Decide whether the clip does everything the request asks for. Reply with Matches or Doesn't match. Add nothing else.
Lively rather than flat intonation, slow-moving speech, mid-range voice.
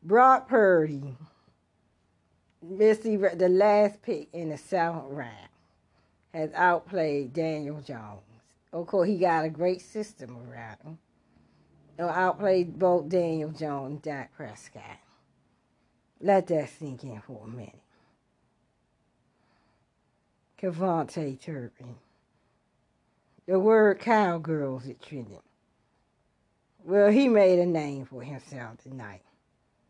Matches